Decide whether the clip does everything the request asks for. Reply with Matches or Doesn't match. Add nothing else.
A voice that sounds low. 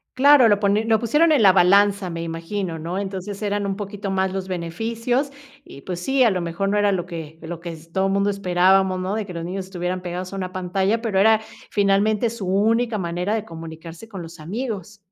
Doesn't match